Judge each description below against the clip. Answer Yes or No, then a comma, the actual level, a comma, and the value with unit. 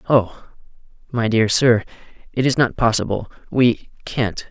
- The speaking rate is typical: No, slow, 105 wpm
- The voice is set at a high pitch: No, low, 115 Hz